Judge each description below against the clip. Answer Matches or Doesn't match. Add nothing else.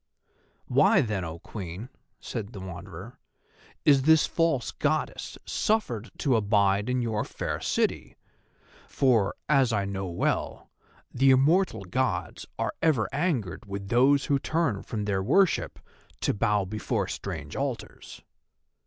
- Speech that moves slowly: Matches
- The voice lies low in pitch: Matches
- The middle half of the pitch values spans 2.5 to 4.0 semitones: Doesn't match